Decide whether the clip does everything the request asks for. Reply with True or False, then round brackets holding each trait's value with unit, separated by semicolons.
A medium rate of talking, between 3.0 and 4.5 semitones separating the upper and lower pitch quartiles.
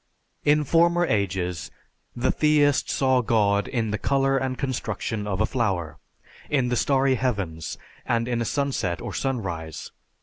False (145 wpm; 5.2 semitones)